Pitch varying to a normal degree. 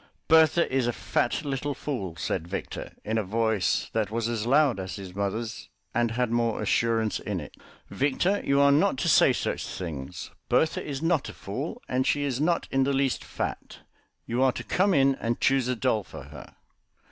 Yes: average, 4.4 semitones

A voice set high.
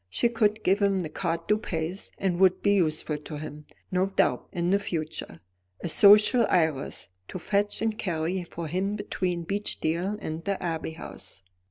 No: medium, 180 Hz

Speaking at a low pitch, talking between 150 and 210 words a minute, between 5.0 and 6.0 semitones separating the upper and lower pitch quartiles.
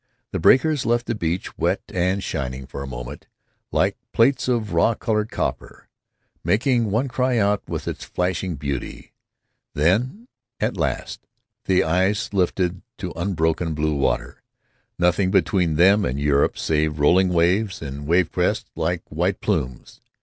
No: very low, 90 Hz; average, 140 wpm; average, 5.3 semitones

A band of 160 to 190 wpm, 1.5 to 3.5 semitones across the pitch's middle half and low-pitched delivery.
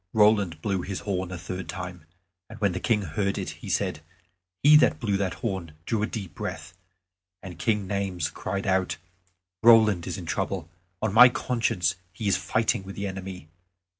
Yes: average, 180 wpm; average, 2.8 semitones; very low, 95 Hz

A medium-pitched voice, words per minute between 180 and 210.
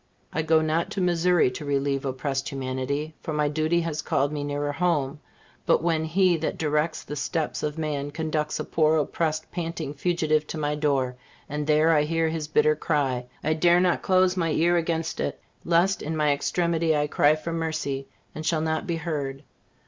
Yes: medium, 155 Hz; average, 190 wpm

